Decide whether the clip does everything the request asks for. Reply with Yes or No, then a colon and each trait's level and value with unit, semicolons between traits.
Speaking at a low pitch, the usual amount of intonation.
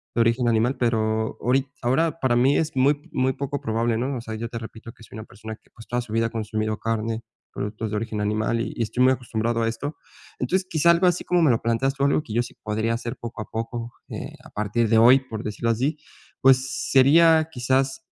Yes: low, 120 Hz; average, 3.1 semitones